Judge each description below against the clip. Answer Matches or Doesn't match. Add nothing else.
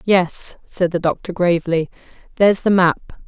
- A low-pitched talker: Doesn't match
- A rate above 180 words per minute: Doesn't match